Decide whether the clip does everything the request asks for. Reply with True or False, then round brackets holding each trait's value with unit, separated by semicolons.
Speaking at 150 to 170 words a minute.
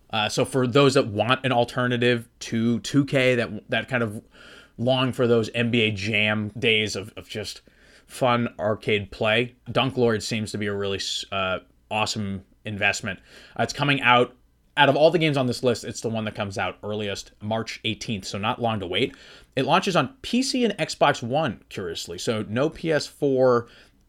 False (180 wpm)